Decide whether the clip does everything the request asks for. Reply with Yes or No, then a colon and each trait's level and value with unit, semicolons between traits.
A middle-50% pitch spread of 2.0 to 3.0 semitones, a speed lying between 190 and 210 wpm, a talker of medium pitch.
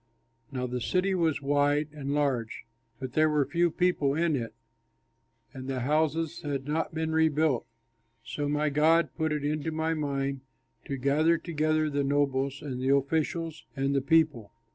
No: narrow, 2.5 semitones; average, 165 wpm; medium, 145 Hz